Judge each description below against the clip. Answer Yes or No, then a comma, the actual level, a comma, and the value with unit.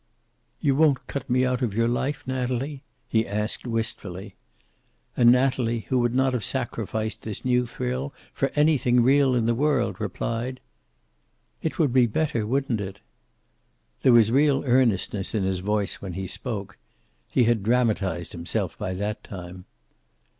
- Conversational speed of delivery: Yes, average, 155 wpm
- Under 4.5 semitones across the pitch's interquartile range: Yes, average, 3.6 semitones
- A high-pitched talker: No, low, 120 Hz